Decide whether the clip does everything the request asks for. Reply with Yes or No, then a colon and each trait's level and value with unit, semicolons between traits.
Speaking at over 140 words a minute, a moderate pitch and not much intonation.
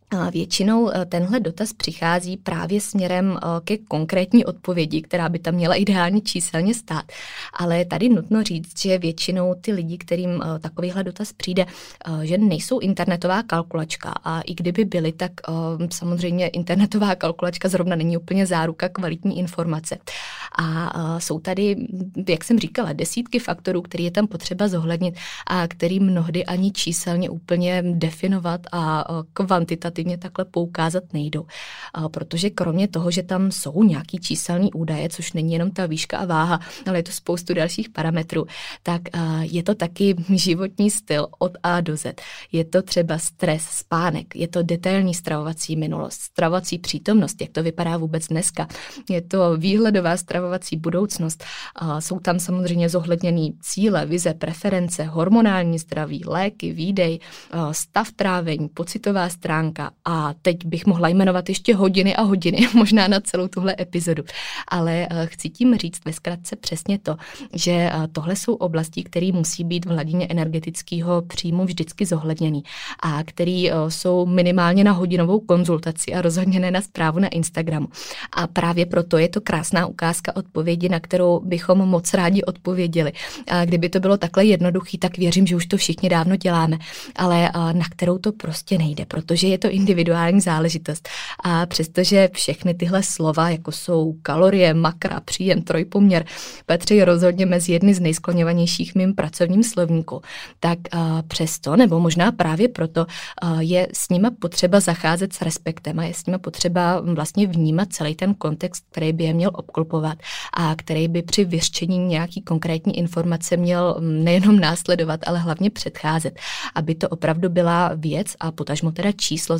Yes: average, 150 wpm; medium, 175 Hz; narrow, 2.1 semitones